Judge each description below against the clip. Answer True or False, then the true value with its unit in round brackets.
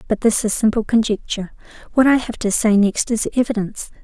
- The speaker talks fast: False (195 wpm)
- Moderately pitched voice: False (220 Hz)